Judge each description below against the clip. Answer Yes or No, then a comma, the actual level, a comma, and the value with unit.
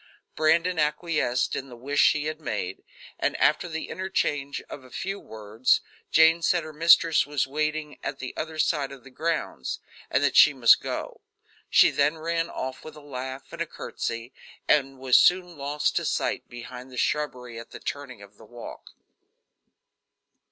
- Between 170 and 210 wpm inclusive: Yes, average, 175 wpm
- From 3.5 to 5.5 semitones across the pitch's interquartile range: Yes, average, 3.8 semitones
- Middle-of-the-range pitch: Yes, medium, 145 Hz